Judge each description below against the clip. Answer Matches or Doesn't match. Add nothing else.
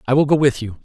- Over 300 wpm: Matches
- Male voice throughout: Matches